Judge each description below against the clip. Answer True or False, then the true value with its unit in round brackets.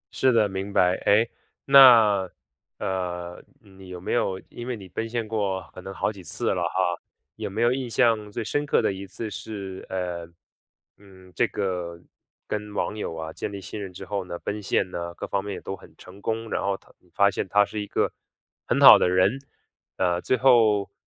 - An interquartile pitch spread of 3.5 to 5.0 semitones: False (2.9 semitones)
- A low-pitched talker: True (100 Hz)